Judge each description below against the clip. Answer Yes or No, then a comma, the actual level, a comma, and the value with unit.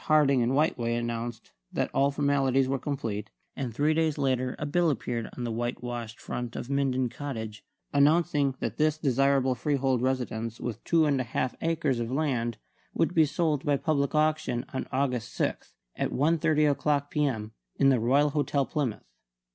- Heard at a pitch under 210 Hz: Yes, low, 135 Hz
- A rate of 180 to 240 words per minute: No, average, 170 wpm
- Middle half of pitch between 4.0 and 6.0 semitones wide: No, average, 3.4 semitones